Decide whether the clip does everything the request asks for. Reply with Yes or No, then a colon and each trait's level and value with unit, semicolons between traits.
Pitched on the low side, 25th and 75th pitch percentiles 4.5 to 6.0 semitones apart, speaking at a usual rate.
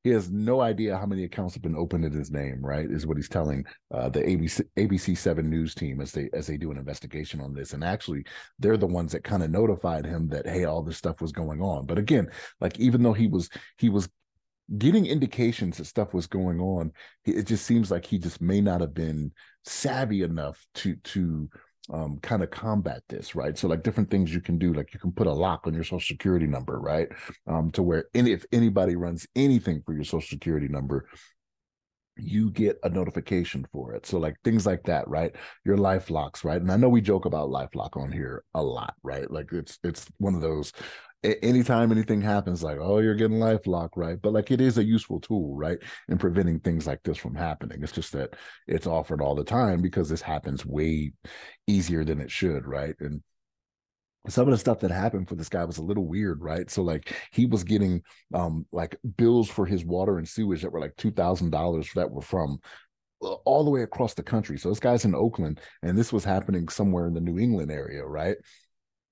No: very low, 90 Hz; average, 4.8 semitones; fast, 220 wpm